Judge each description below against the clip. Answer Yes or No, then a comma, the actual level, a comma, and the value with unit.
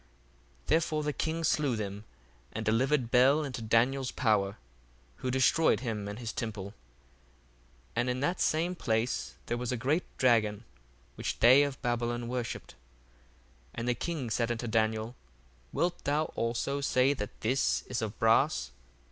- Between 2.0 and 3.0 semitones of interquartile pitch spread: No, average, 3.6 semitones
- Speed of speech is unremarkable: Yes, average, 155 wpm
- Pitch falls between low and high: No, low, 120 Hz